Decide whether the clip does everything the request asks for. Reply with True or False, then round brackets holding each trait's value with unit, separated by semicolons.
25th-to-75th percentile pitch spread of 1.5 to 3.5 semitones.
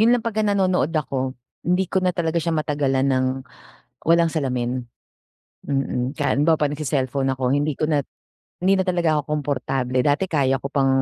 False (4.0 semitones)